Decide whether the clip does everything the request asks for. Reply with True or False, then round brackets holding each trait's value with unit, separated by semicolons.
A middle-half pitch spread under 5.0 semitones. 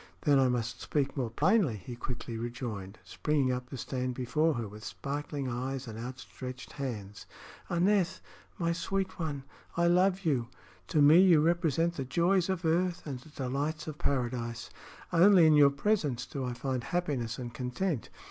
False (5.3 semitones)